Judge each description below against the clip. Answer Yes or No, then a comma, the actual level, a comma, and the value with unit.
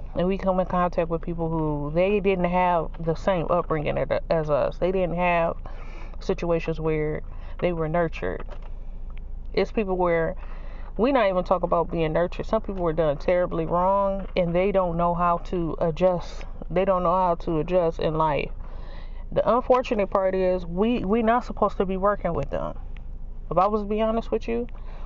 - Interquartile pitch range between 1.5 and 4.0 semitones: Yes, average, 2.7 semitones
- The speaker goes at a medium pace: Yes, average, 180 wpm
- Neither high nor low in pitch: Yes, medium, 180 Hz